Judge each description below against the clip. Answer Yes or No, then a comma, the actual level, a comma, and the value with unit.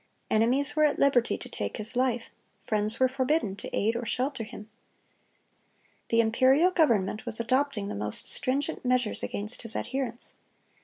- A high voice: Yes, high, 245 Hz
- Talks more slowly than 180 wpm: Yes, average, 155 wpm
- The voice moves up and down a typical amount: Yes, average, 3.8 semitones